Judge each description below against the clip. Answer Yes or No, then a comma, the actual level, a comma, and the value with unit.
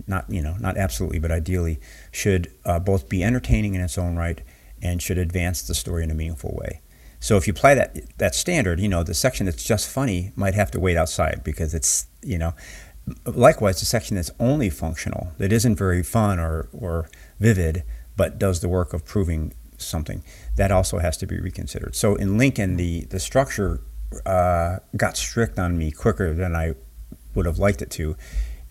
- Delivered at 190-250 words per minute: Yes, average, 195 wpm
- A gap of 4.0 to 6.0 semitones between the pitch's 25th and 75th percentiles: No, average, 3.6 semitones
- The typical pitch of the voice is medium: No, very low, 90 Hz